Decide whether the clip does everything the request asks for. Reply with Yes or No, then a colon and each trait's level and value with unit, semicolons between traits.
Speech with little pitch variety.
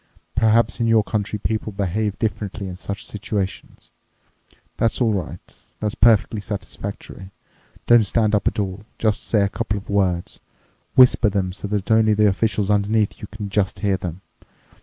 Yes: narrow, 1.8 semitones